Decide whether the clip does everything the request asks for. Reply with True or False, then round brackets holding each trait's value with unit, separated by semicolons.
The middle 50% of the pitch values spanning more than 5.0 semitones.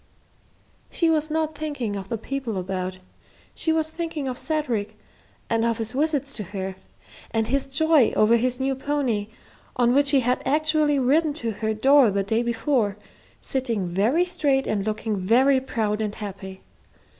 True (5.4 semitones)